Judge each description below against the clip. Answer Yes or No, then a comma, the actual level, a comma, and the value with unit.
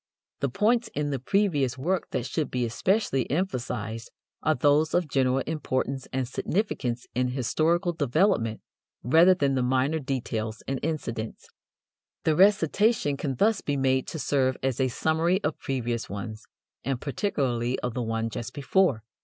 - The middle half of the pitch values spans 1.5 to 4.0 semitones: No, average, 4.6 semitones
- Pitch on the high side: No, low, 135 Hz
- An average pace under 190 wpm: Yes, average, 155 wpm